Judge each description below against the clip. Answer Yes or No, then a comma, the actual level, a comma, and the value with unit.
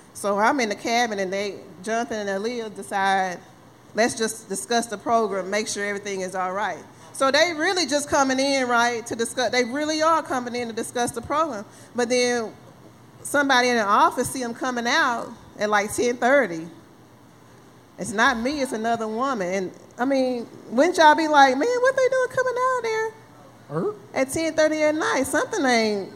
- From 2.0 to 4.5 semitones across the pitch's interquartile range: No, average, 5.3 semitones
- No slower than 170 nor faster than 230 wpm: Yes, average, 190 wpm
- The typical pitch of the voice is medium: No, high, 245 Hz